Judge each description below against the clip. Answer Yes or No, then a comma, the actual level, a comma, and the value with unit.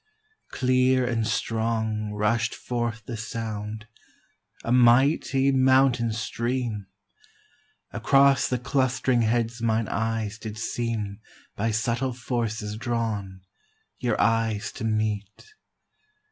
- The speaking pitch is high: No, low, 115 Hz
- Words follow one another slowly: Yes, slow, 100 wpm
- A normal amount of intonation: No, narrow, 2.2 semitones